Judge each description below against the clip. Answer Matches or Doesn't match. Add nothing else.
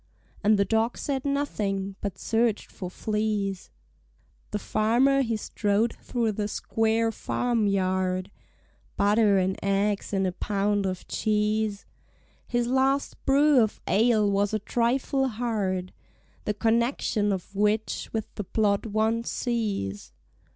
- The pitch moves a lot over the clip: Doesn't match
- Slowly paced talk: Matches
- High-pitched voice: Matches